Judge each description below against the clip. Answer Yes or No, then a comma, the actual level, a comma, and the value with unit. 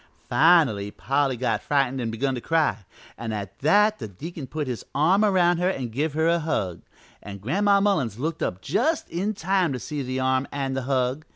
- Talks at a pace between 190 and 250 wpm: Yes, average, 200 wpm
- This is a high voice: No, medium, 140 Hz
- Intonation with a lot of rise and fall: Yes, wide, 5.7 semitones